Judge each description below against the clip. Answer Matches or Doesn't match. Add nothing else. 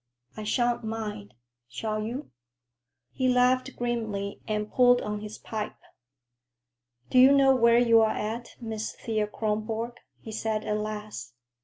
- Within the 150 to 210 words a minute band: Doesn't match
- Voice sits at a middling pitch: Doesn't match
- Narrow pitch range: Matches